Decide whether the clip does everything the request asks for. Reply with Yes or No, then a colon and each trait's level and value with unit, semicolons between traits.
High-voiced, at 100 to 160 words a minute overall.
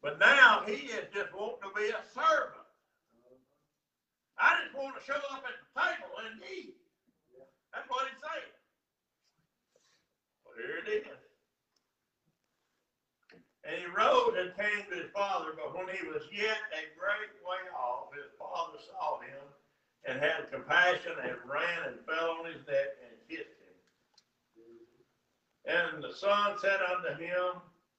Yes: high, 210 Hz; average, 150 wpm